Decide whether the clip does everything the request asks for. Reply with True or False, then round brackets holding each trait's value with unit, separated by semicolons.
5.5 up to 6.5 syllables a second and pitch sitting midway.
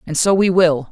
False (5.1 syllables/s; 175 Hz)